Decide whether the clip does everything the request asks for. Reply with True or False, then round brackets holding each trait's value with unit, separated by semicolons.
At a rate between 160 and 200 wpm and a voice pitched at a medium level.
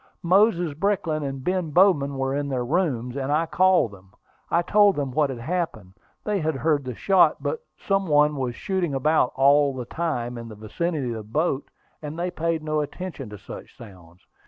True (195 wpm; 150 Hz)